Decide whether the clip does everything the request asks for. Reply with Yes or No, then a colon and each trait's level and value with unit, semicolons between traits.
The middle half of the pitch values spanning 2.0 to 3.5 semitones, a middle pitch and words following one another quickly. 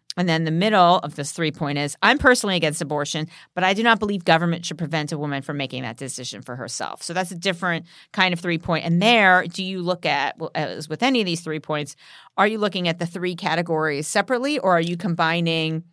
Yes: average, 3.1 semitones; medium, 170 Hz; fast, 235 wpm